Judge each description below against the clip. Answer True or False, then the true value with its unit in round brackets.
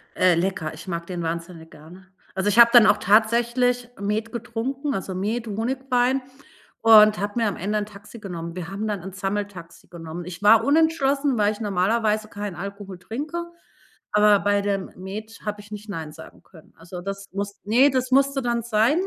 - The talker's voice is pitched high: True (205 Hz)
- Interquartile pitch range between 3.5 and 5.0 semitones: True (3.8 semitones)